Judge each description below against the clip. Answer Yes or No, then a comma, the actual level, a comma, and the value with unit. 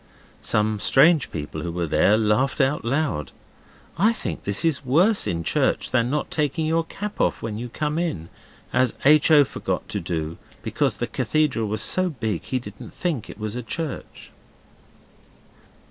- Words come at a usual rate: Yes, average, 170 wpm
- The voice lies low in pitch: Yes, low, 130 Hz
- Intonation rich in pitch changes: Yes, wide, 6.7 semitones